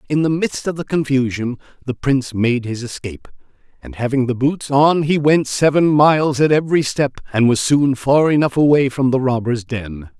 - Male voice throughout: Yes, male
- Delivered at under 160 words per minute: No, average, 195 wpm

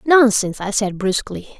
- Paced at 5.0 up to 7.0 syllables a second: No, 4.7 syllables/s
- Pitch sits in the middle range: No, high, 215 Hz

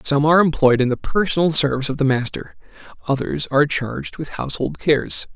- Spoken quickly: No, average, 180 wpm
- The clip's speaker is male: Yes, male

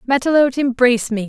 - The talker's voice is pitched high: Yes, very high, 255 Hz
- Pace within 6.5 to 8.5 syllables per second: Yes, 7.2 syllables/s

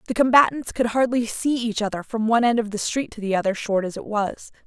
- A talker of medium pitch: No, high, 225 Hz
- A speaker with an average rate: No, fast, 255 wpm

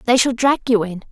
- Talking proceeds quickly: Yes, fast, 270 wpm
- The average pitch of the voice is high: Yes, high, 235 Hz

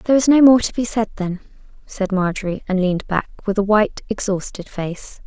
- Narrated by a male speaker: No, female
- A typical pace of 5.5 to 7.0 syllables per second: Yes, 5.6 syllables/s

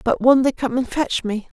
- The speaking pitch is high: Yes, very high, 250 Hz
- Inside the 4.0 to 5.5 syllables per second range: Yes, 4.9 syllables/s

